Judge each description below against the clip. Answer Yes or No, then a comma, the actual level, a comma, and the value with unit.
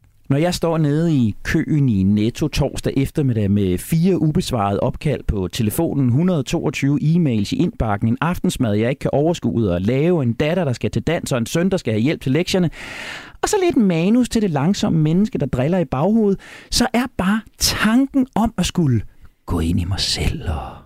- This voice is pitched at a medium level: Yes, medium, 145 Hz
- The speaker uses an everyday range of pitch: No, wide, 7.5 semitones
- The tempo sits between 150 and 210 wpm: Yes, average, 195 wpm